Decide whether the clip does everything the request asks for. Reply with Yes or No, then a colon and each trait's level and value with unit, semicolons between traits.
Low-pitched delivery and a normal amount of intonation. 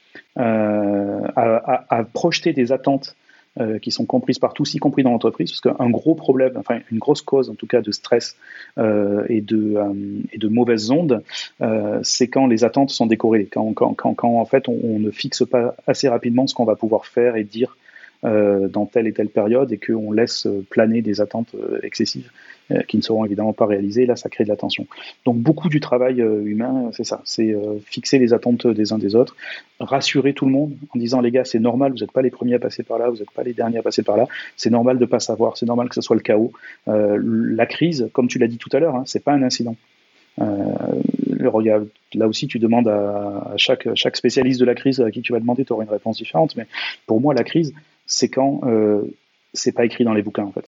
Yes: low, 120 Hz; average, 3.0 semitones